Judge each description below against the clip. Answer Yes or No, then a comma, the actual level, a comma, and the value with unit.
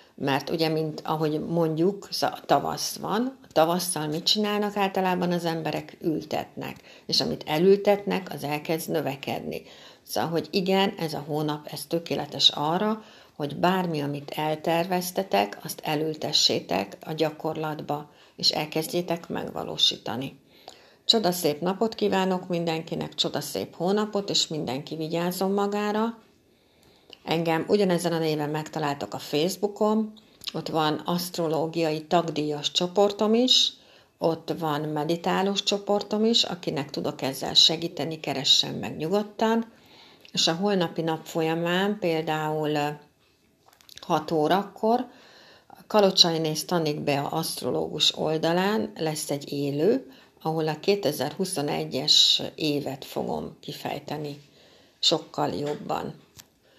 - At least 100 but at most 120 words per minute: Yes, average, 110 wpm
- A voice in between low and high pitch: Yes, medium, 165 Hz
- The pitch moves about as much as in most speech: Yes, average, 4.1 semitones